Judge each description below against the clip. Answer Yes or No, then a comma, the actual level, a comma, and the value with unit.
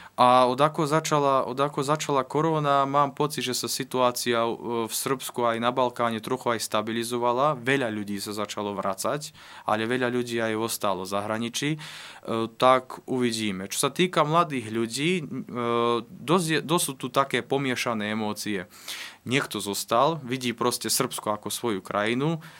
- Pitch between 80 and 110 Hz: No, low, 125 Hz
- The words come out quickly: No, average, 145 wpm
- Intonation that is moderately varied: Yes, average, 3.7 semitones